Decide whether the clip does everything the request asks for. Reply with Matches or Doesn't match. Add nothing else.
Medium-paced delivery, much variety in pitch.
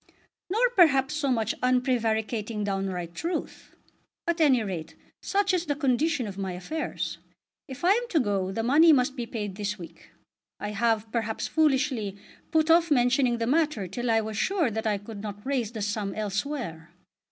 Matches